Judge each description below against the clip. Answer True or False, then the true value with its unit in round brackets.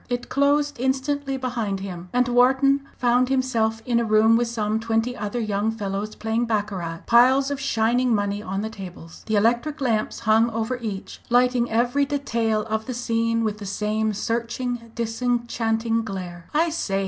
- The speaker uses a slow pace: False (165 wpm)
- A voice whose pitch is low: False (230 Hz)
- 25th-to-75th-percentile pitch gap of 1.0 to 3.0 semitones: True (2.7 semitones)